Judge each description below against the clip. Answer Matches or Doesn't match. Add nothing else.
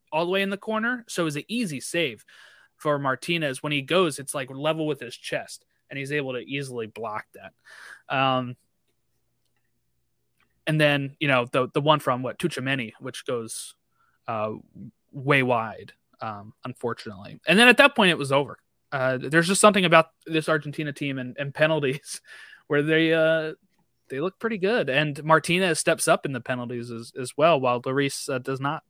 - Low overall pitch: Doesn't match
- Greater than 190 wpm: Doesn't match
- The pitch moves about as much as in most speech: Matches